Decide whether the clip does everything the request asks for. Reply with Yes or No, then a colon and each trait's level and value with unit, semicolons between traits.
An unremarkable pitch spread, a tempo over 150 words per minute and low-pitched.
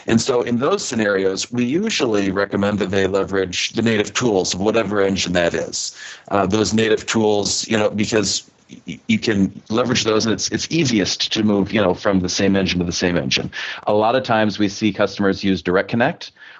No: narrow, 2.1 semitones; fast, 205 wpm; low, 100 Hz